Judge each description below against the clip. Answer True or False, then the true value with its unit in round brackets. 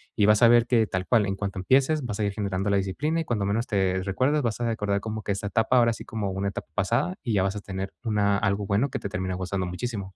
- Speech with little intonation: False (3.1 semitones)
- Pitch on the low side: True (105 Hz)